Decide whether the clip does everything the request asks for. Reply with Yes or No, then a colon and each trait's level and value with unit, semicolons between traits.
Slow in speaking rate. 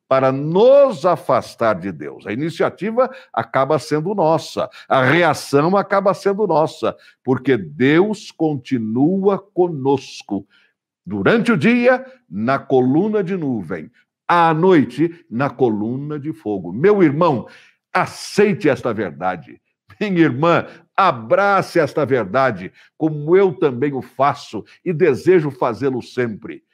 Yes: slow, 115 wpm